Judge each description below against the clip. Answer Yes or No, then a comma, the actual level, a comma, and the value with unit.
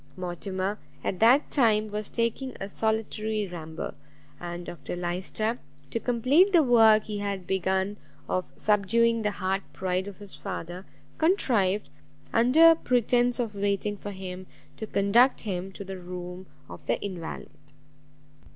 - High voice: Yes, high, 205 Hz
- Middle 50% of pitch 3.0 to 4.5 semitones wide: Yes, average, 3.7 semitones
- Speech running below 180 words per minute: Yes, average, 140 wpm